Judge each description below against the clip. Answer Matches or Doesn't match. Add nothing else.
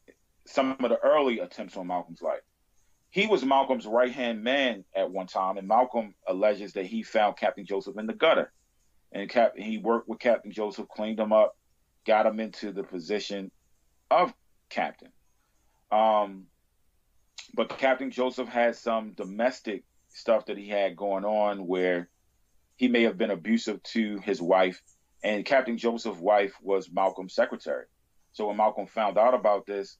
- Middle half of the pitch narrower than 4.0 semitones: Matches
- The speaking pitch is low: Matches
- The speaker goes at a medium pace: Matches